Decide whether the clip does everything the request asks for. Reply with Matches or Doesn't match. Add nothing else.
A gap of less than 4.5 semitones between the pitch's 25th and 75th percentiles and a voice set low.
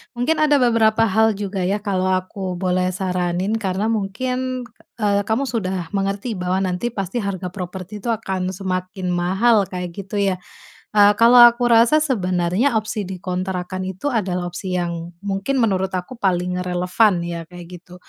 Doesn't match